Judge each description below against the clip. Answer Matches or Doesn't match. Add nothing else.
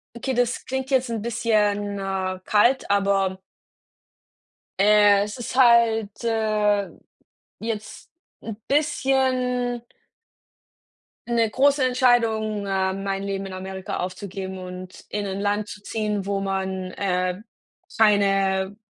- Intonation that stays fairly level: Doesn't match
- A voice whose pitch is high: Matches